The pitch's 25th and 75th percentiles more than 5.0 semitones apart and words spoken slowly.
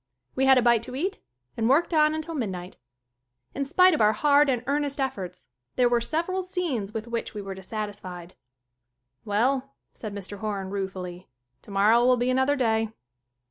No: wide, 5.4 semitones; average, 175 wpm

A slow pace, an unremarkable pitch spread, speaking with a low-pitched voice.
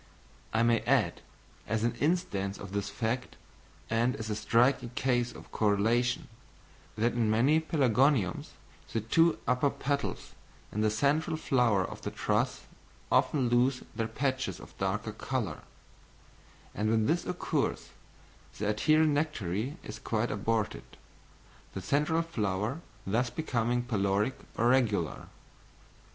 Yes: slow, 130 wpm; average, 4.3 semitones; low, 120 Hz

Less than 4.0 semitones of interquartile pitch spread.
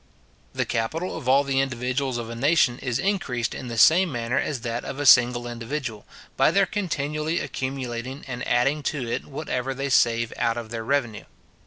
Yes: average, 3.2 semitones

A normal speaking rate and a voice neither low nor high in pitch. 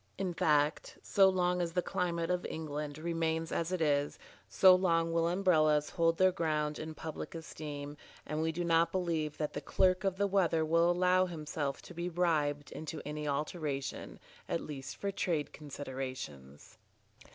Yes: average, 165 wpm; medium, 160 Hz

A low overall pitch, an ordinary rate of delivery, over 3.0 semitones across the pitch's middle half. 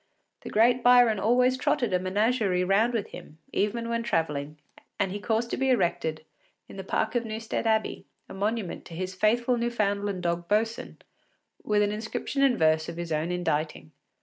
No: high, 210 Hz; average, 175 wpm; average, 4.6 semitones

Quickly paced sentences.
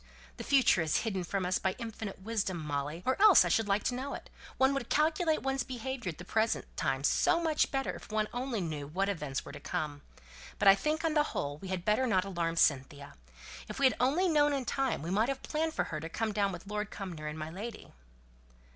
Yes: fast, 235 wpm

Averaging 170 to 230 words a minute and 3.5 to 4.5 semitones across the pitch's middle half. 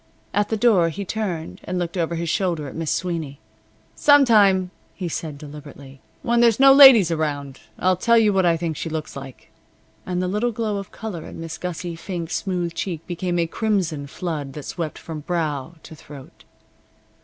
Yes: average, 190 wpm; average, 4.0 semitones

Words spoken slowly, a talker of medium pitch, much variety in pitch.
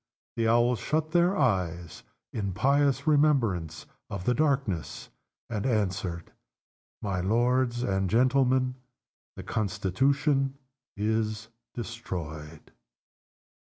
No: slow, 90 wpm; low, 115 Hz; wide, 5.9 semitones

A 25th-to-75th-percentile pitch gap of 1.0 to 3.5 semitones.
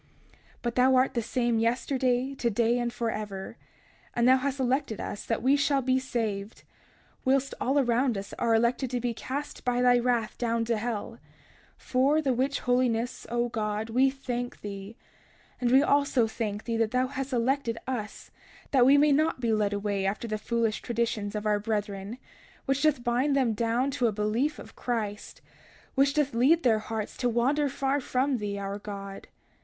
Yes: average, 3.1 semitones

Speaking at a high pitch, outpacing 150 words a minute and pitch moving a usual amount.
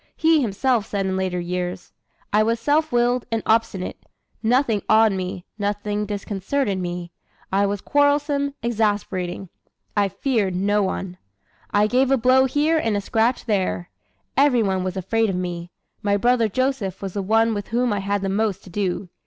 Yes: high, 210 Hz; average, 170 wpm; average, 4.1 semitones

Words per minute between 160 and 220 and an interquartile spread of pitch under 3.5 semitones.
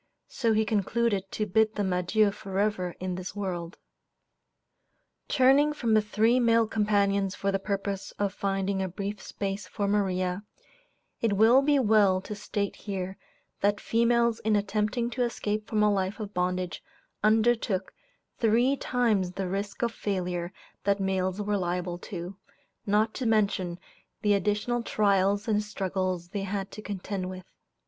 No: average, 150 wpm; narrow, 2.4 semitones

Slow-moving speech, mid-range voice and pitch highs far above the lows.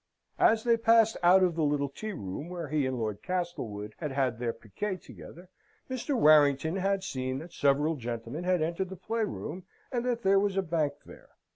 No: average, 195 wpm; medium, 165 Hz; wide, 6.1 semitones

